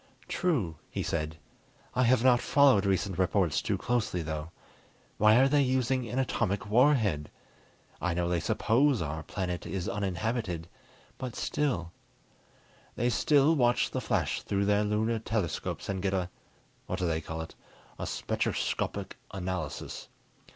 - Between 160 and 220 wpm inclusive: No, average, 145 wpm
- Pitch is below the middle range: Yes, low, 100 Hz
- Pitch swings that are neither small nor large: No, wide, 5.8 semitones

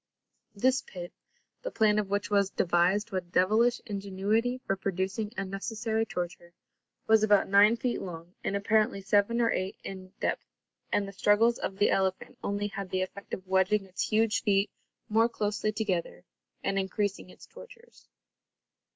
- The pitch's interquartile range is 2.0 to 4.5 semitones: Yes, narrow, 2.5 semitones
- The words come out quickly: No, average, 155 wpm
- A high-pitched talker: Yes, high, 200 Hz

